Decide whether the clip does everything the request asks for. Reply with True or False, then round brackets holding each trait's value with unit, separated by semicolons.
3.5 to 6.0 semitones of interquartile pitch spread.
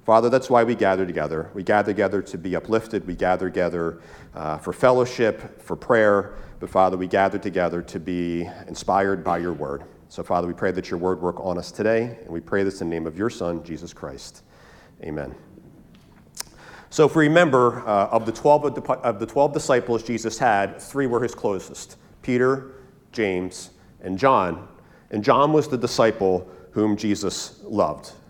True (5.2 semitones)